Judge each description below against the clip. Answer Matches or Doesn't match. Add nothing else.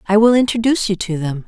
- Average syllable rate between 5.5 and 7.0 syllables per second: Matches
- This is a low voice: Doesn't match